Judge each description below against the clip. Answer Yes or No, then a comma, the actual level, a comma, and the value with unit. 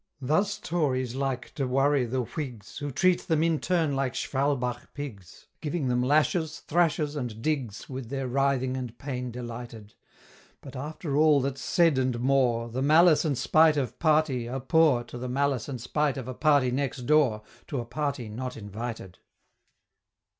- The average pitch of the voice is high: No, low, 135 Hz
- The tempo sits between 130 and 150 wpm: No, average, 170 wpm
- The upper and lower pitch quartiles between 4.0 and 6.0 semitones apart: No, average, 3.4 semitones